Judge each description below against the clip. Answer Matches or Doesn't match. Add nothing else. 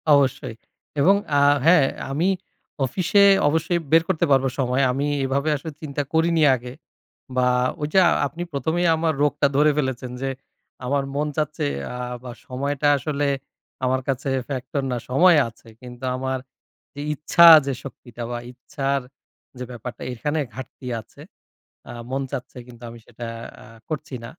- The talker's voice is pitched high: Doesn't match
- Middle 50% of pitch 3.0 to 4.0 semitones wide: Matches